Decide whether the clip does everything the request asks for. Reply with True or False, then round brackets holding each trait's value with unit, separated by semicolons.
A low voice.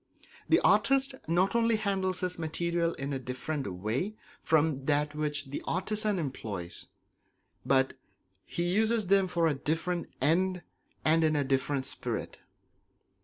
False (165 Hz)